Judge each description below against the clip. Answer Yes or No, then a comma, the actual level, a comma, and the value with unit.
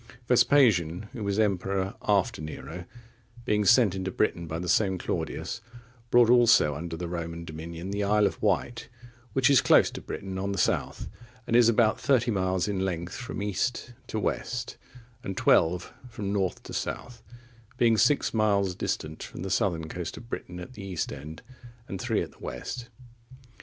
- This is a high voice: No, low, 100 Hz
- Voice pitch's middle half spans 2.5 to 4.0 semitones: No, average, 4.6 semitones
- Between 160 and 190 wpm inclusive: Yes, average, 175 wpm